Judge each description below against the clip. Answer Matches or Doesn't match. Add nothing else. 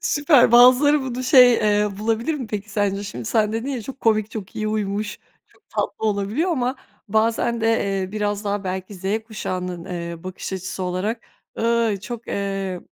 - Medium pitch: Doesn't match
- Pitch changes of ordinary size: Matches